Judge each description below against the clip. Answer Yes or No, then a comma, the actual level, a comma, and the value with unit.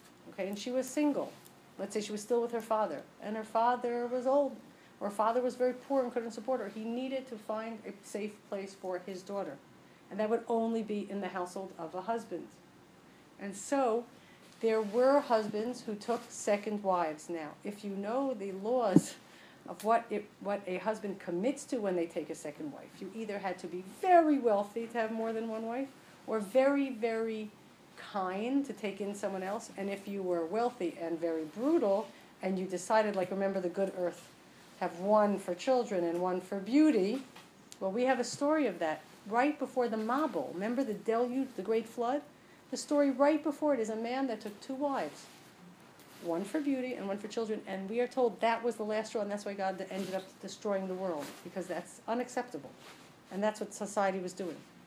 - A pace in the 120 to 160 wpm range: No, fast, 205 wpm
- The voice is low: No, high, 215 Hz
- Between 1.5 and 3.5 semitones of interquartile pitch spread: No, average, 4.2 semitones